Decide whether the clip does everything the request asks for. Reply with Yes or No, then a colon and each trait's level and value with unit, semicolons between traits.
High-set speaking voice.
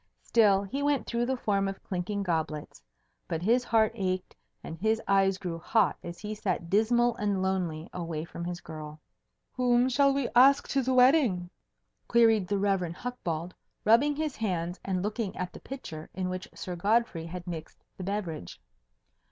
Yes: high, 195 Hz